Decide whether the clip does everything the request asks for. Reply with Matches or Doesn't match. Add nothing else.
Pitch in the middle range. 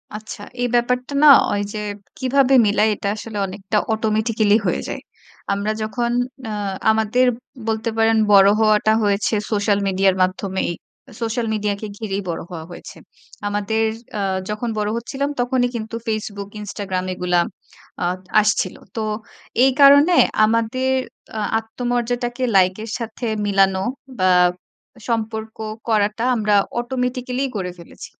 Doesn't match